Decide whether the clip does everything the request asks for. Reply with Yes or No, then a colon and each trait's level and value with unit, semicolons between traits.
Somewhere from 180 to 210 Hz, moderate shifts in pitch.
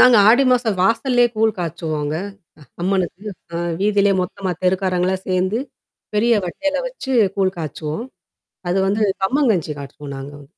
Yes: high, 190 Hz; average, 4.5 semitones